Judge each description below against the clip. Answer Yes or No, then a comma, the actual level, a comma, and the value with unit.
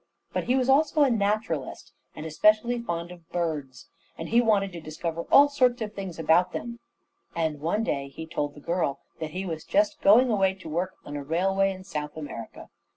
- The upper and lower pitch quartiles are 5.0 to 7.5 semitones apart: Yes, wide, 5.5 semitones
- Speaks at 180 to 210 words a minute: Yes, average, 200 wpm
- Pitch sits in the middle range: Yes, medium, 180 Hz